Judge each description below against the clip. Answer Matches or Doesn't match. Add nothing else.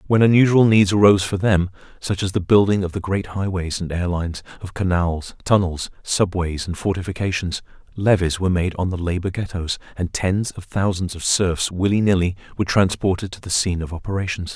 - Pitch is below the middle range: Matches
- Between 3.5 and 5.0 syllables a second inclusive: Doesn't match